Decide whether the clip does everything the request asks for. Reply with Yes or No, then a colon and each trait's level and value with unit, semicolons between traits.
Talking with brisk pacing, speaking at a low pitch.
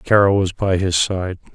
No: average, 195 wpm; very low, 95 Hz